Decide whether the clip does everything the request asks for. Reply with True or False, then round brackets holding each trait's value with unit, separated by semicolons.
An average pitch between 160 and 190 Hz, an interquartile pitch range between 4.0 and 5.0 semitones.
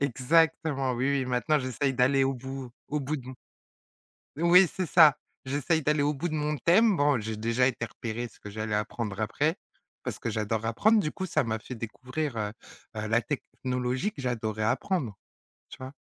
False (130 Hz; 4.6 semitones)